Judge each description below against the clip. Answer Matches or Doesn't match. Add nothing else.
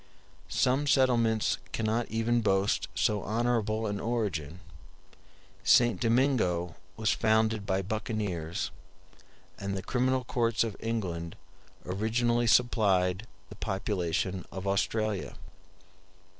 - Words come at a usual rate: Doesn't match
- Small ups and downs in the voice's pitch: Doesn't match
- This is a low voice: Matches